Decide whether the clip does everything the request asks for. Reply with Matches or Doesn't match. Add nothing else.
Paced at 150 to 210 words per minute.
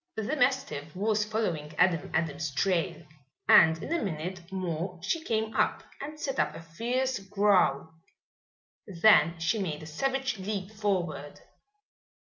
Doesn't match